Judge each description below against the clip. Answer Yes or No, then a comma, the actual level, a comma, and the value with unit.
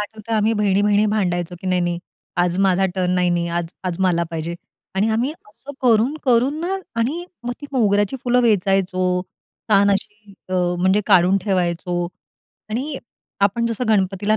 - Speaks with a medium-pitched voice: No, high, 200 Hz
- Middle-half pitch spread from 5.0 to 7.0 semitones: No, average, 3.8 semitones